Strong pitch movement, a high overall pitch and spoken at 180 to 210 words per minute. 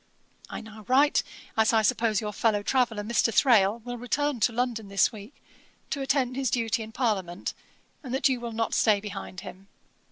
No: average, 3.0 semitones; high, 225 Hz; average, 185 wpm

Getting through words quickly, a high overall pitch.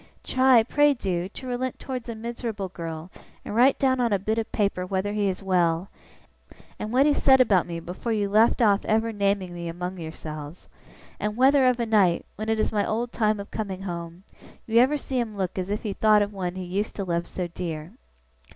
Yes: fast, 215 wpm; high, 205 Hz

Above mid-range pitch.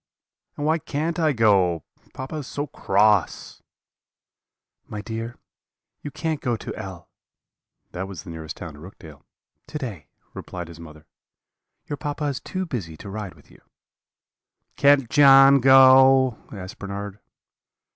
No: low, 115 Hz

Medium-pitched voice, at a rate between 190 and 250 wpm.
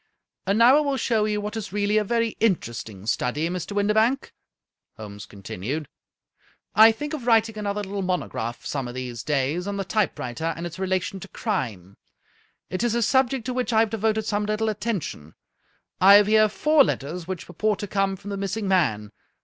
No: high, 200 Hz; average, 200 wpm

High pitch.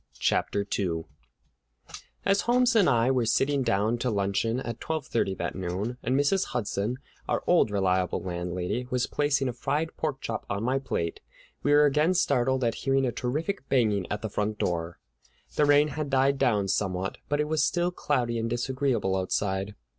No: low, 125 Hz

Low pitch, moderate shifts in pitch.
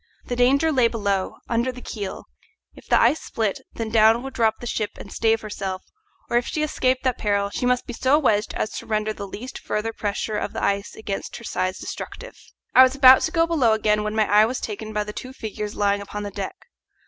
No: high, 220 Hz; average, 3.3 semitones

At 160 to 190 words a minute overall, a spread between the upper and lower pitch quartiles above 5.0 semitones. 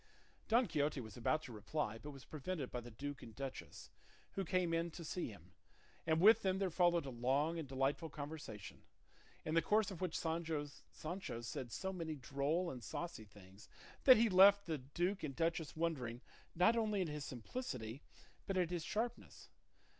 Yes: average, 180 wpm; wide, 5.5 semitones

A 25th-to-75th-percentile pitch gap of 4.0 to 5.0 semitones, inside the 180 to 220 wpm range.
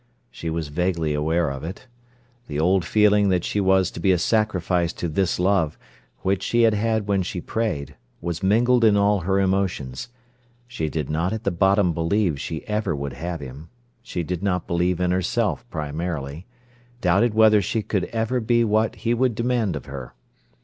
Yes: average, 4.4 semitones; average, 185 wpm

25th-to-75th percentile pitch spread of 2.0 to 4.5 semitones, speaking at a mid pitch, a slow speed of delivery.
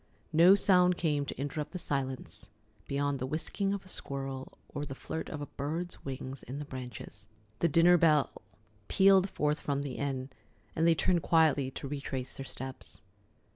No: average, 3.8 semitones; medium, 145 Hz; average, 175 wpm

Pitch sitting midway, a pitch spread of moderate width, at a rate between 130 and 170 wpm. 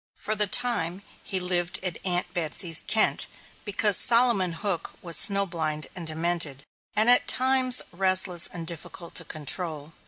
Yes: medium, 180 Hz; average, 3.8 semitones; average, 150 wpm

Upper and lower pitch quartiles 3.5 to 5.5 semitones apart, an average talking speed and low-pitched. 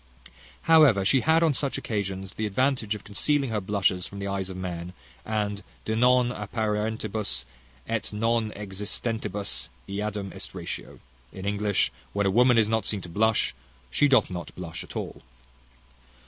No: average, 2.8 semitones; average, 160 wpm; low, 105 Hz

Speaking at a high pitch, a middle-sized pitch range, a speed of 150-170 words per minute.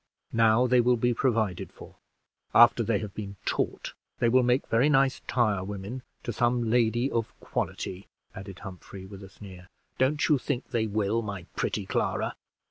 No: low, 115 Hz; average, 3.5 semitones; average, 165 wpm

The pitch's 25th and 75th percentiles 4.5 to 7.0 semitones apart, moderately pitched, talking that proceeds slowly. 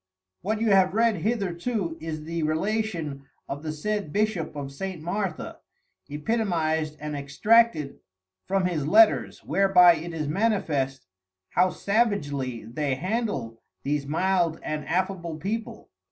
Yes: average, 5.2 semitones; medium, 170 Hz; slow, 125 wpm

